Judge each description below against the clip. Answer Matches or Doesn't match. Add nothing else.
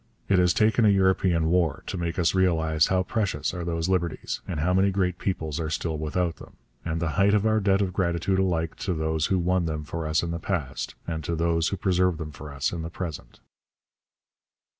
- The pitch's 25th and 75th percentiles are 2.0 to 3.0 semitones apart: Matches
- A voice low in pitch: Matches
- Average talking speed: Doesn't match